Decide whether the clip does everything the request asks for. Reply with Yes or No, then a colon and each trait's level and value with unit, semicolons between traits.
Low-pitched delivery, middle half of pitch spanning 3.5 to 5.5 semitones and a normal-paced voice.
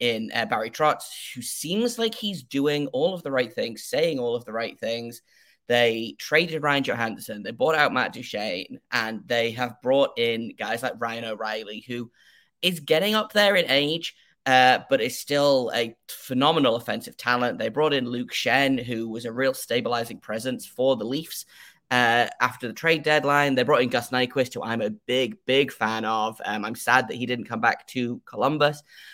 Yes: low, 125 Hz; average, 3.8 semitones; average, 195 wpm